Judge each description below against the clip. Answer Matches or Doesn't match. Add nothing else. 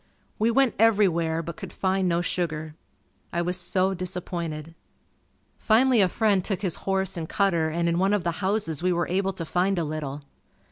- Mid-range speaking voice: Matches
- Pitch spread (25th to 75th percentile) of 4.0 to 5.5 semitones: Doesn't match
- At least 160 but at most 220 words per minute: Matches